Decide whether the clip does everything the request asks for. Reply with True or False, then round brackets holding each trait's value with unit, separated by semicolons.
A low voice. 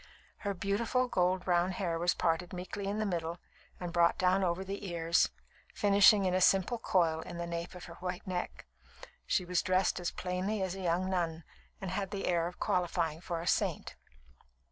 False (180 Hz)